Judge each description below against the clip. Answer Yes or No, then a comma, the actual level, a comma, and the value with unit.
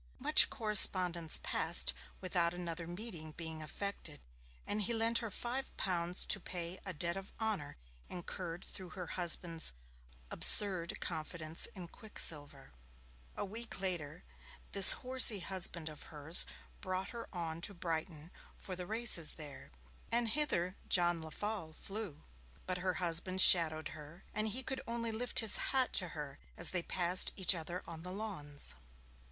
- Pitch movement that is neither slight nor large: Yes, average, 3.8 semitones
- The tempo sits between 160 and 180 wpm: No, average, 145 wpm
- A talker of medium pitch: Yes, medium, 180 Hz